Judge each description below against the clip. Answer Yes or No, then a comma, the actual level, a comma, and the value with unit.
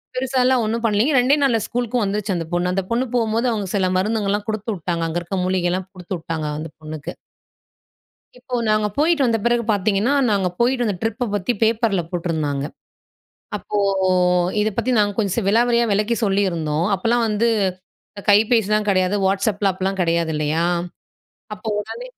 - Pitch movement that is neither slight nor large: Yes, average, 4.2 semitones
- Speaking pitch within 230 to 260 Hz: No, high, 205 Hz